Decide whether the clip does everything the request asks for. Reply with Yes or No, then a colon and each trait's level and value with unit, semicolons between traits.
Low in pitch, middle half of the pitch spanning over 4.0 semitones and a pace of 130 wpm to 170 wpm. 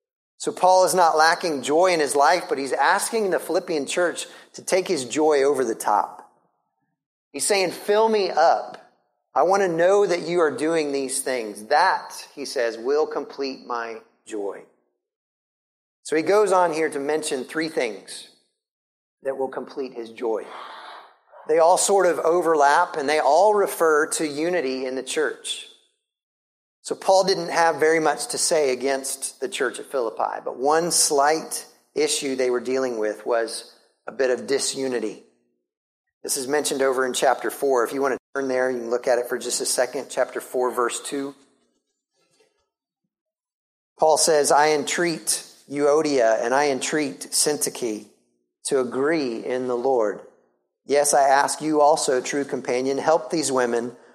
No: medium, 145 Hz; wide, 5.6 semitones; average, 165 wpm